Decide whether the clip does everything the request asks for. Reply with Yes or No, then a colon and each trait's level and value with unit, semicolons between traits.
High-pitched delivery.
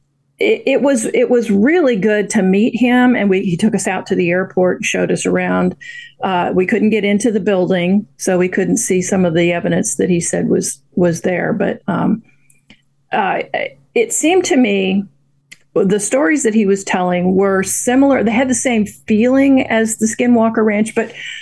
Yes: high, 210 Hz